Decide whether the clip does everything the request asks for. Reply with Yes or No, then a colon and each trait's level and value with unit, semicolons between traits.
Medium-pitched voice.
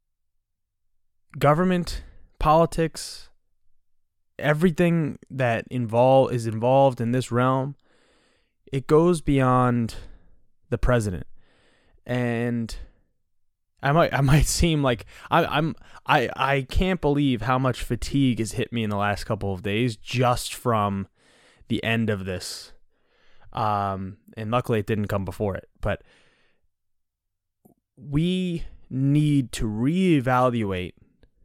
No: low, 120 Hz